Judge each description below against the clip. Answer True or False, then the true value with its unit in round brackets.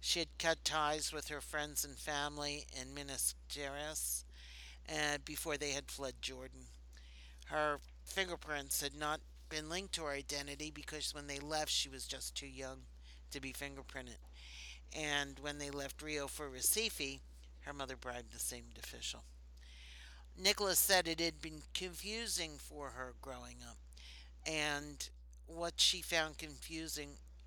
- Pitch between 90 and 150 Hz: True (140 Hz)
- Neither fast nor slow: True (145 wpm)